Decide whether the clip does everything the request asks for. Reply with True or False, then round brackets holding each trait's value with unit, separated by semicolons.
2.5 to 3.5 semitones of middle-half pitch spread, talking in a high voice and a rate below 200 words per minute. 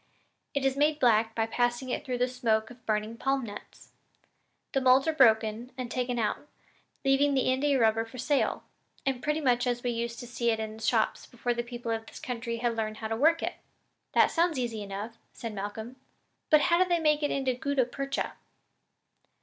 False (3.1 semitones; 245 Hz; 205 wpm)